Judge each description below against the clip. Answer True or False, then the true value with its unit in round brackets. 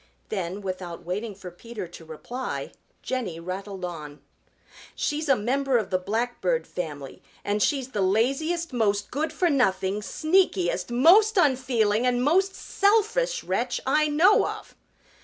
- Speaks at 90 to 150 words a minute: True (140 wpm)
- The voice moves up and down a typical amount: False (8.2 semitones)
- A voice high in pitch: True (235 Hz)